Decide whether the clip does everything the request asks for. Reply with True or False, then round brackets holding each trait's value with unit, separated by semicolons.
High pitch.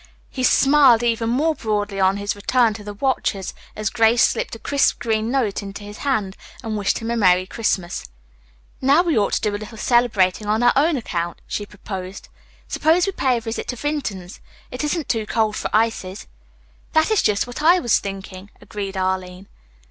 True (220 Hz)